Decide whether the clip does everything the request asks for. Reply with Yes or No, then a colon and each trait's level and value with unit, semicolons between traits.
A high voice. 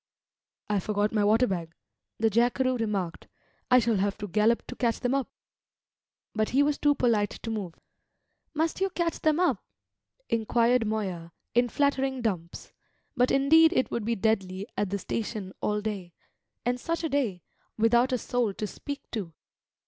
Yes: high, 225 Hz